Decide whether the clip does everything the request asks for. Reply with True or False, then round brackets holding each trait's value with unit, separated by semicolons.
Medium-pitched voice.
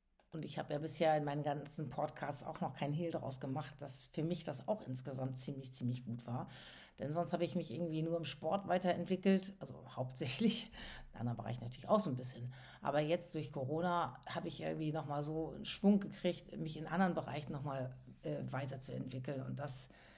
True (150 Hz)